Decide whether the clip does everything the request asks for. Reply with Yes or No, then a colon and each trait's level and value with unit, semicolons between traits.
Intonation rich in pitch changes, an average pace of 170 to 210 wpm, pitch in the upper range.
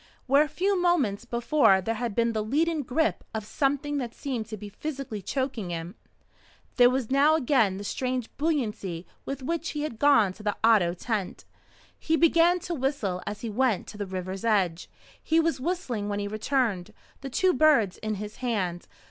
Yes: wide, 6.0 semitones; average, 185 wpm; high, 240 Hz